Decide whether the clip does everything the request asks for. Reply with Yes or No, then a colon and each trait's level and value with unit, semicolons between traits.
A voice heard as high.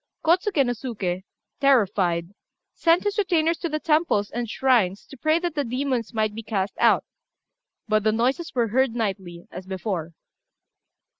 Yes: high, 235 Hz